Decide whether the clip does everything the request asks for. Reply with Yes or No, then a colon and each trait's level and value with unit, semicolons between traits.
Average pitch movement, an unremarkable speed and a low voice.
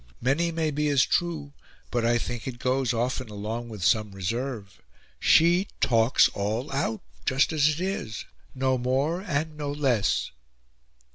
Yes: average, 4.6 semitones; average, 150 wpm; low, 130 Hz